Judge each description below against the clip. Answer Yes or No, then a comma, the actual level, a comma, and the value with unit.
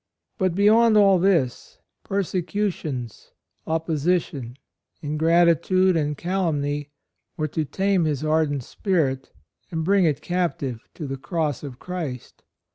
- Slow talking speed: Yes, slow, 120 wpm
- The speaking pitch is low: No, medium, 160 Hz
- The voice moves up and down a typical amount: Yes, average, 4.3 semitones